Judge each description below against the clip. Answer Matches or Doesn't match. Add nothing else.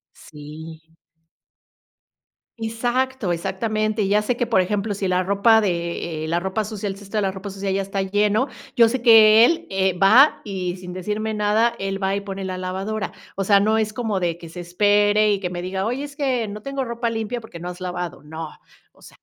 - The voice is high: Matches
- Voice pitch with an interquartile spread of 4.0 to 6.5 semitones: Doesn't match